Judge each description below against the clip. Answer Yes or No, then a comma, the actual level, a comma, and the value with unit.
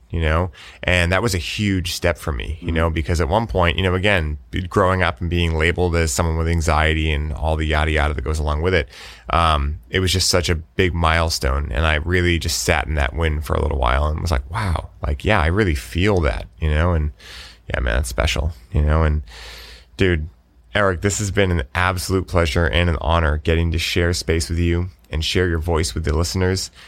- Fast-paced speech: Yes, fast, 230 wpm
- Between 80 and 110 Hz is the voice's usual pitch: Yes, very low, 85 Hz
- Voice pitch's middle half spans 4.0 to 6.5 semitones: No, narrow, 2.6 semitones